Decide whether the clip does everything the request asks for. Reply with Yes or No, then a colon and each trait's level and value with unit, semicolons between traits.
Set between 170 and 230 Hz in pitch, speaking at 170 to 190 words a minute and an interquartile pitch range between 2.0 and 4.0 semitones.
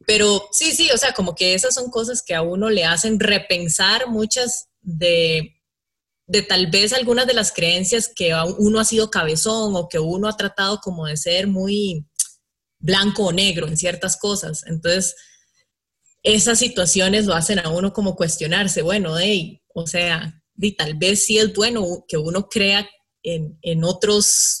Yes: high, 190 Hz; average, 175 wpm; average, 3.7 semitones